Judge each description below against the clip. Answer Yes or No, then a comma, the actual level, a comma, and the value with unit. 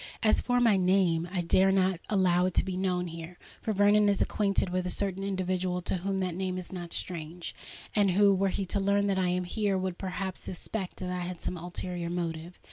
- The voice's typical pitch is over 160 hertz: Yes, medium, 185 Hz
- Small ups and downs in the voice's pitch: Yes, narrow, 1.7 semitones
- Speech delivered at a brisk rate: Yes, fast, 215 wpm